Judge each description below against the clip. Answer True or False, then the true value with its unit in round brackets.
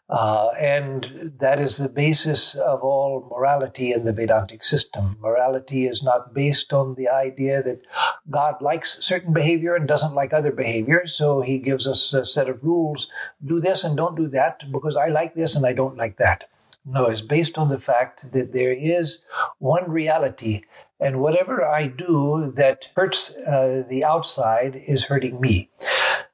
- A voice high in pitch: False (140 Hz)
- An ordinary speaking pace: True (175 wpm)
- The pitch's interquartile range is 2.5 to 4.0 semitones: True (3.1 semitones)